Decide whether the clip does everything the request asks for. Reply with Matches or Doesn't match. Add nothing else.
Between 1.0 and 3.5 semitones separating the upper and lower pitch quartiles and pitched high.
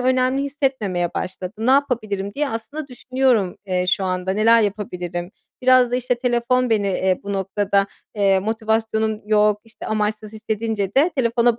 Doesn't match